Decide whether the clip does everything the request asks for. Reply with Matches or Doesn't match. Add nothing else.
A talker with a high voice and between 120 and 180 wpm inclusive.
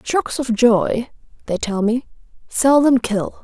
Matches